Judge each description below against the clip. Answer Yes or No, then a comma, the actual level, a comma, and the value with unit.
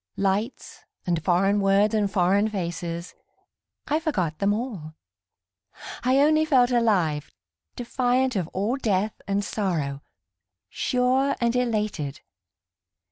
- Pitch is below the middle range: No, high, 205 Hz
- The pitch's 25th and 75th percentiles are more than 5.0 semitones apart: Yes, wide, 5.5 semitones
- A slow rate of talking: Yes, slow, 110 wpm